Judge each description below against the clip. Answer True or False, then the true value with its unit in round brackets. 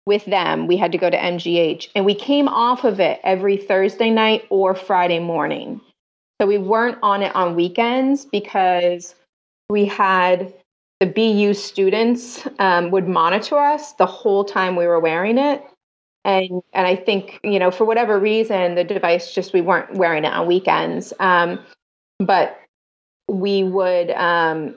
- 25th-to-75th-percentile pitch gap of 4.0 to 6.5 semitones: False (2.9 semitones)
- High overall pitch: True (195 Hz)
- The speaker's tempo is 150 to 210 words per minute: True (160 wpm)